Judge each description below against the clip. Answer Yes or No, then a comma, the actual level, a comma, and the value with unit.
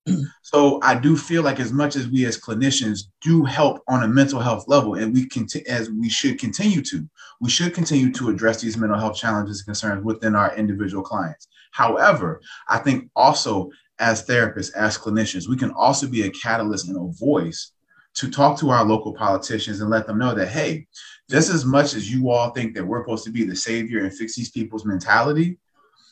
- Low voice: Yes, low, 120 Hz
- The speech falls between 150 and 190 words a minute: No, fast, 205 wpm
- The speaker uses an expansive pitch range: No, average, 4.7 semitones